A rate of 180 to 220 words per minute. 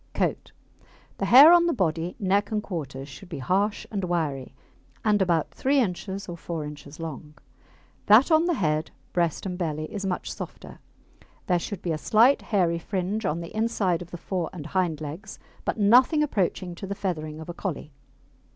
Yes: average, 185 wpm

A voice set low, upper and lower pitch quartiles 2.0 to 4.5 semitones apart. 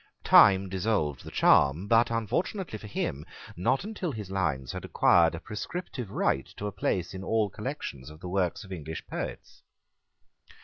No: very low, 95 Hz; wide, 5.4 semitones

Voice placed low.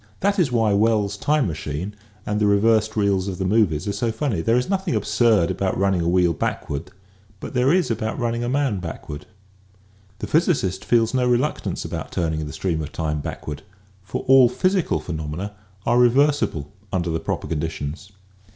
Yes: low, 105 Hz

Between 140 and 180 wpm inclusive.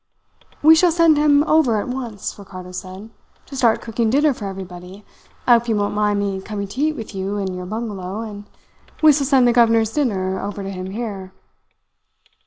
No: average, 195 wpm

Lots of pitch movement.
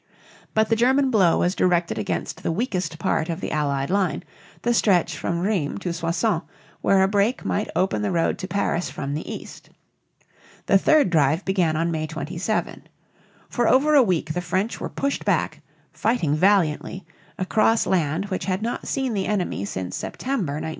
No: average, 4.7 semitones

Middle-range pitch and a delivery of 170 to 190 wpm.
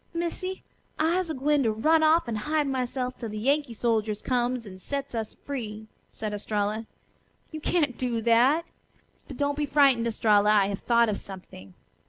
No: high, 245 Hz; average, 175 wpm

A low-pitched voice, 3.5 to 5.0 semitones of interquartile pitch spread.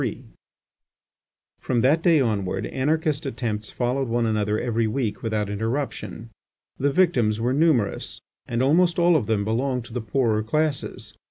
Yes: low, 120 Hz; average, 4.4 semitones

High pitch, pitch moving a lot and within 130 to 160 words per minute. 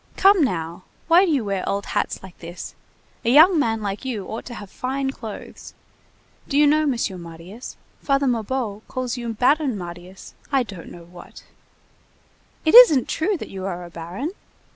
No: high, 230 Hz; wide, 6.7 semitones; average, 175 wpm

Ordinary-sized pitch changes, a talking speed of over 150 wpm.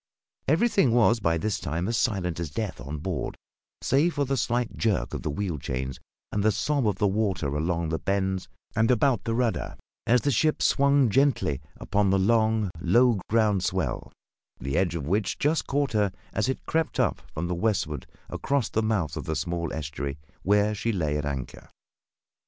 No: wide, 5.8 semitones; average, 185 wpm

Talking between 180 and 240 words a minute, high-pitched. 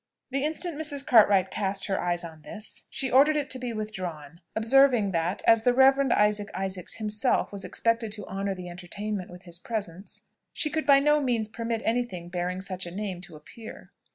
Yes: average, 195 wpm; high, 210 Hz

